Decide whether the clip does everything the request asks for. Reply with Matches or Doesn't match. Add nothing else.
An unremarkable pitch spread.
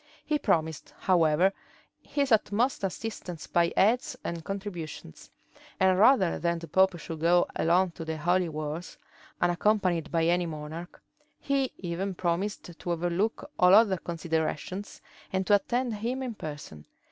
Matches